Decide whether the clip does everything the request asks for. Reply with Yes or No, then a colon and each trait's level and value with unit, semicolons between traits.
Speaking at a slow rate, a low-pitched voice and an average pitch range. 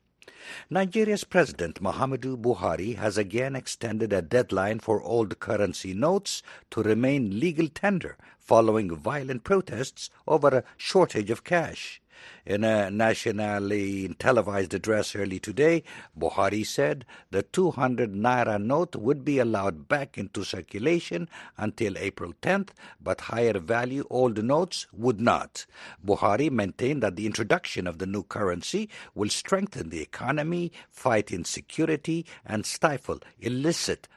No: slow, 130 wpm; low, 115 Hz; wide, 6.6 semitones